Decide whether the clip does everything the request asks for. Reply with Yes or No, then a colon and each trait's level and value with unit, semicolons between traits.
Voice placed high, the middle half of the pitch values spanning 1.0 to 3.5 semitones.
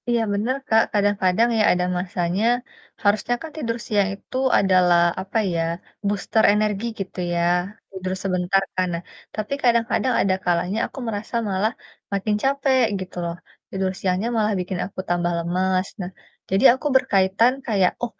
Yes: high, 195 Hz; average, 3.2 semitones